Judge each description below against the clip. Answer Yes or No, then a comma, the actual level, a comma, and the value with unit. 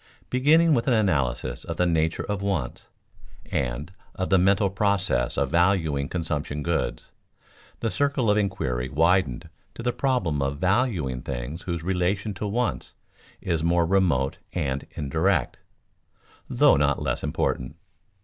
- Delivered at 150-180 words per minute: No, average, 140 wpm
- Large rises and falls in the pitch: Yes, wide, 5.7 semitones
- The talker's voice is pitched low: Yes, very low, 85 Hz